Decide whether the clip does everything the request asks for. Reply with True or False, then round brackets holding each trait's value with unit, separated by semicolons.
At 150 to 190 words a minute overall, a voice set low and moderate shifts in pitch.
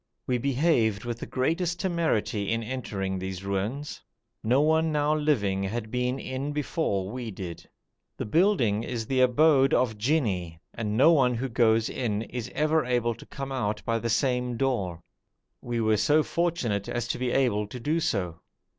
True (170 wpm; 120 Hz; 4.8 semitones)